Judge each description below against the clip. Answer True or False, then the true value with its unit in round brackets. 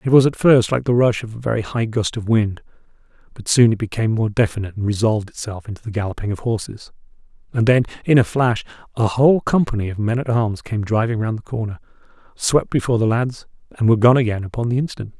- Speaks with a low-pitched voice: True (115 Hz)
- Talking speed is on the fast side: True (220 wpm)